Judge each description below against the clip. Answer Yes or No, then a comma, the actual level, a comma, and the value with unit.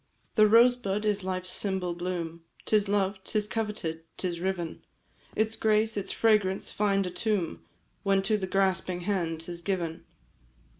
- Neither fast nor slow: Yes, average, 145 wpm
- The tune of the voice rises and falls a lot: No, average, 2.9 semitones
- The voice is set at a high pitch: Yes, high, 195 Hz